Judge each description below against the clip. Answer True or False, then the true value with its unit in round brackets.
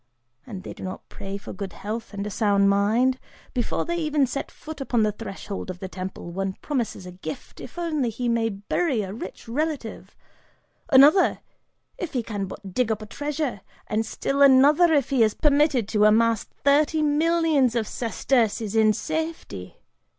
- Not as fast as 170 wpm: False (175 wpm)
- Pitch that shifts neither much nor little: False (6.0 semitones)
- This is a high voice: True (230 Hz)